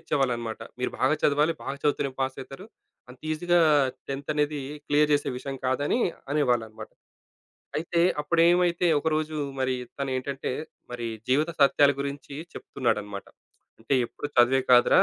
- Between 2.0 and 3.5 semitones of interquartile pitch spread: Yes, average, 2.9 semitones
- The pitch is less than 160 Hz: Yes, medium, 140 Hz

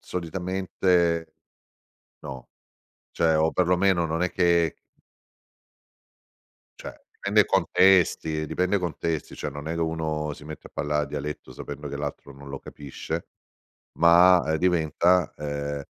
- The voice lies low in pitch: Yes, very low, 80 Hz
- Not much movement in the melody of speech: No, average, 3.1 semitones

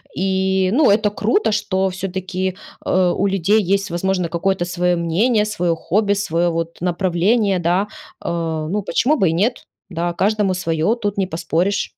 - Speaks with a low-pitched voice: No, high, 190 Hz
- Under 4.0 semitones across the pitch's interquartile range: Yes, average, 2.8 semitones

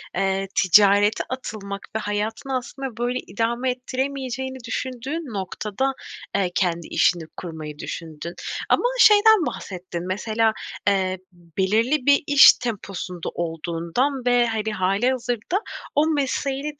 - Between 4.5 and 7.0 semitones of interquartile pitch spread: Yes, wide, 5.6 semitones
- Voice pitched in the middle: No, high, 225 Hz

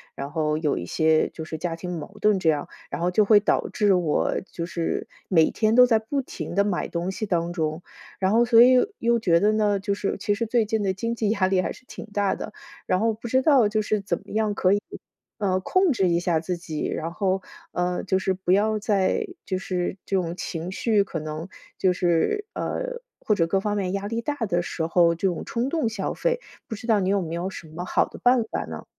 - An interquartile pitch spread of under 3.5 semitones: No, average, 4.0 semitones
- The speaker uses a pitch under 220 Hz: Yes, high, 195 Hz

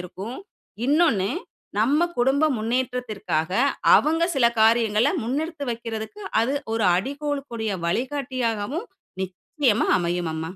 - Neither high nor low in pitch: No, high, 235 Hz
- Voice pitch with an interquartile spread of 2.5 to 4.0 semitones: No, average, 5.0 semitones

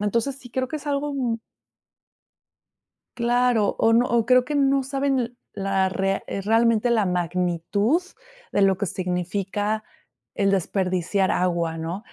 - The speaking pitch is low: No, high, 210 Hz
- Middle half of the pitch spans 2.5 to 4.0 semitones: No, average, 4.7 semitones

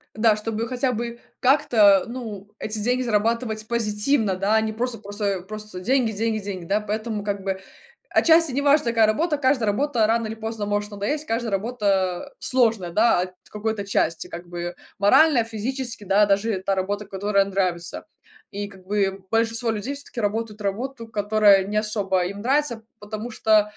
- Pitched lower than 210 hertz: No, high, 215 Hz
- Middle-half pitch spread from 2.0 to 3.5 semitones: Yes, narrow, 2.6 semitones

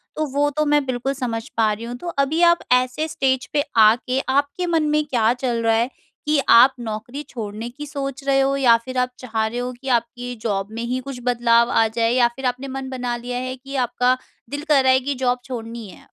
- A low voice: No, very high, 250 Hz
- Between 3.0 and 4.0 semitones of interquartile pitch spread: No, narrow, 2.6 semitones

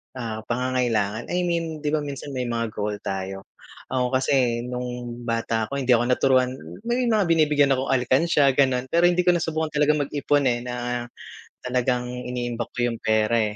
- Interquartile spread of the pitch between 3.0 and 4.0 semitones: Yes, average, 3.5 semitones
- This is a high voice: No, low, 125 Hz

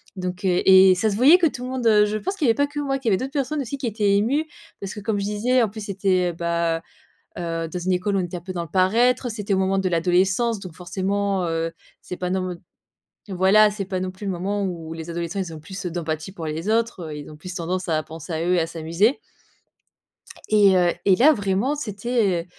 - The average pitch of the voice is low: No, high, 190 Hz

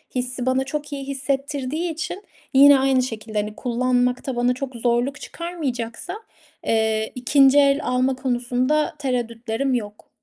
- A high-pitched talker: Yes, very high, 255 Hz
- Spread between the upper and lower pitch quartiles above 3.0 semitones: No, narrow, 2.4 semitones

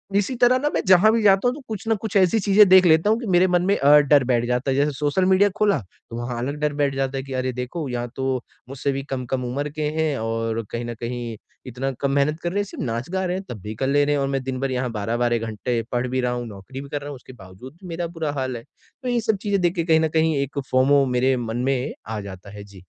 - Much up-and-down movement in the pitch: Yes, wide, 5.9 semitones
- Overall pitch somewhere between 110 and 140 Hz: Yes, low, 135 Hz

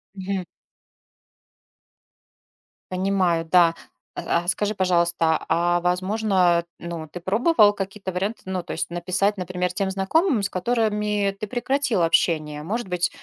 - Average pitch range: Yes, average, 3.0 semitones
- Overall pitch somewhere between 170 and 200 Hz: Yes, medium, 185 Hz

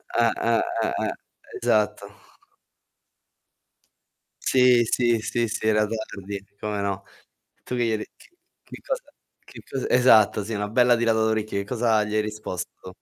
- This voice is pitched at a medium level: No, low, 110 Hz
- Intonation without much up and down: Yes, narrow, 2.2 semitones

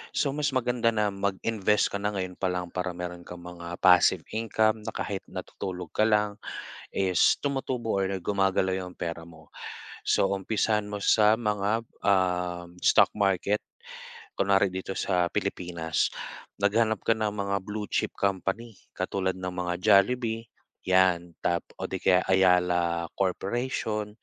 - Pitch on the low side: Yes, very low, 95 Hz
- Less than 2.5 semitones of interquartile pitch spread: No, average, 2.9 semitones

